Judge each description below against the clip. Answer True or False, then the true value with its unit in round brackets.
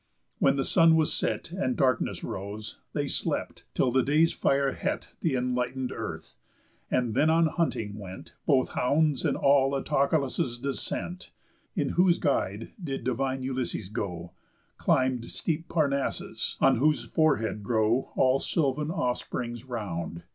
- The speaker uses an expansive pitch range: False (4.2 semitones)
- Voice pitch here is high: False (130 Hz)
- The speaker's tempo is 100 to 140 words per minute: True (135 wpm)